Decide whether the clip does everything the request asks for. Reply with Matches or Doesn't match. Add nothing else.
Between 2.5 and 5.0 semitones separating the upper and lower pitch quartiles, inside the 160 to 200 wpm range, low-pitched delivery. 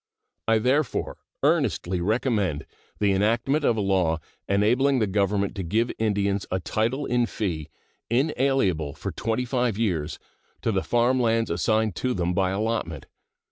Doesn't match